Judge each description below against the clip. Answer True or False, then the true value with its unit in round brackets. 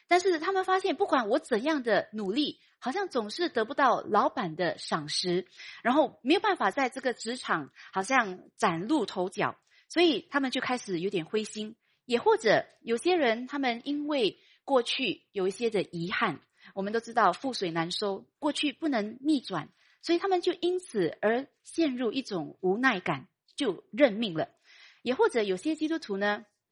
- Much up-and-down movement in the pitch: True (7.6 semitones)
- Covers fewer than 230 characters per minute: False (260 characters per minute)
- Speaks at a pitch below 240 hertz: False (255 Hz)